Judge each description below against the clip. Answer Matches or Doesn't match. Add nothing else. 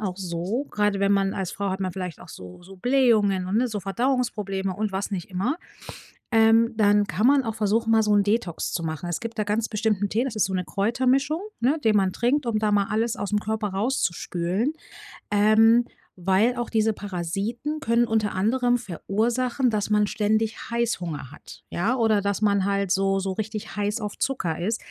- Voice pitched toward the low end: Doesn't match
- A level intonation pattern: Doesn't match